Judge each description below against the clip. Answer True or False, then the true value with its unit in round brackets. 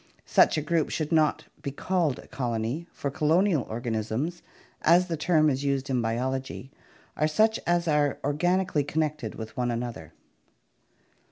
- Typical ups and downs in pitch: True (4.6 semitones)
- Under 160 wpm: True (150 wpm)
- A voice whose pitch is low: False (145 Hz)